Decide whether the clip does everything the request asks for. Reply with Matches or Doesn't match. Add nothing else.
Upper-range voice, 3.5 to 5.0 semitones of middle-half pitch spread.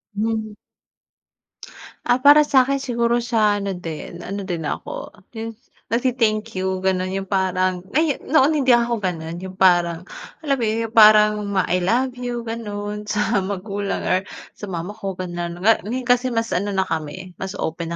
Matches